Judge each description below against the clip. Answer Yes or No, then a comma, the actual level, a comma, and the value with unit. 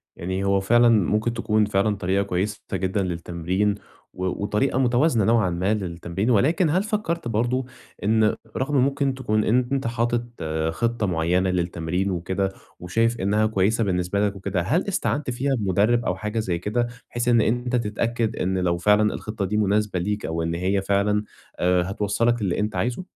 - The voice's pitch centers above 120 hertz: No, low, 105 Hz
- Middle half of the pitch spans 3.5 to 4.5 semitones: Yes, average, 4.1 semitones